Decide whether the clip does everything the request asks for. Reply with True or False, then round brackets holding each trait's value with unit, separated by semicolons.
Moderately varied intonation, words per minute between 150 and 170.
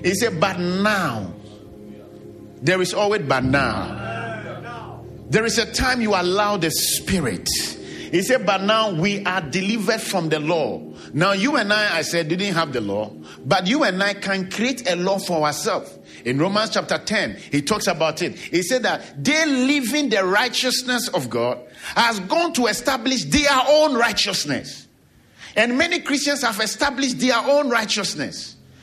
False (6.0 semitones; 165 wpm)